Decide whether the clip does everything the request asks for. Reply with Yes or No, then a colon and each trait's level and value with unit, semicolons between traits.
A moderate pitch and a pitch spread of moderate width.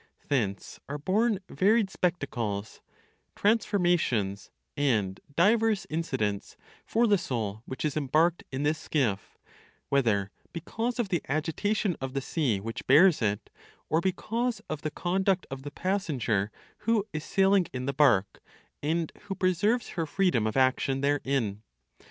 No: medium, 155 Hz; wide, 7.3 semitones